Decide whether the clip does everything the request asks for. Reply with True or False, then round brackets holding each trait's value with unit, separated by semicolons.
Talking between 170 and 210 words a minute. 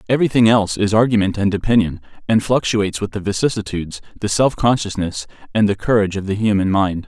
True (180 wpm)